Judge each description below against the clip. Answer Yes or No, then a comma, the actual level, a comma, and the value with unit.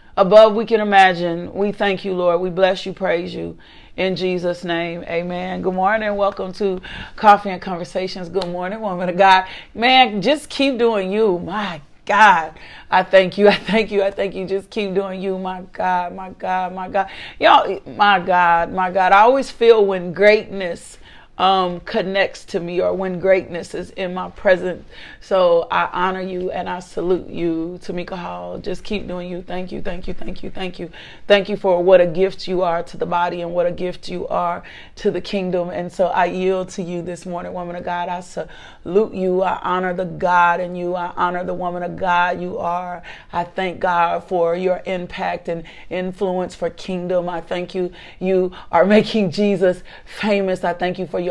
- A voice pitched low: No, medium, 185 Hz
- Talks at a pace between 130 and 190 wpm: No, average, 200 wpm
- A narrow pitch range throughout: Yes, narrow, 1.5 semitones